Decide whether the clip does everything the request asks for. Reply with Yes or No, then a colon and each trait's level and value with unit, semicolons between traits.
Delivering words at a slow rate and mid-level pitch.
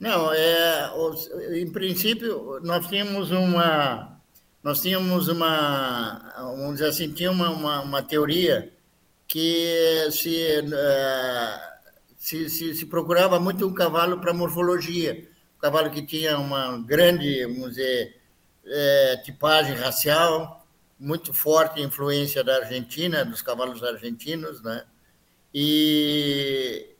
Yes: slow, 110 wpm; medium, 155 Hz